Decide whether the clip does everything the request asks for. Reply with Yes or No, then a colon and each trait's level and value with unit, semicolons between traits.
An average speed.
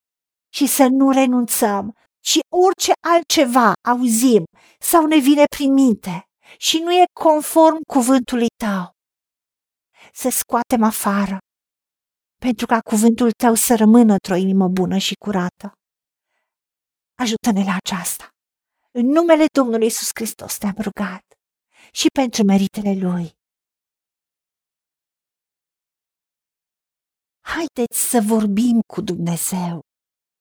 No: slow, 105 wpm